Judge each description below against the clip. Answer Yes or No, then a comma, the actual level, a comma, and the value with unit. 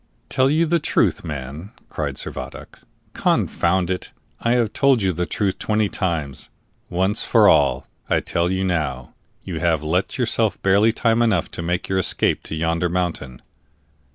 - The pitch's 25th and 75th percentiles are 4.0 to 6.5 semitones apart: Yes, average, 4.7 semitones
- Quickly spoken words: No, average, 160 wpm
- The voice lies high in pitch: No, very low, 90 Hz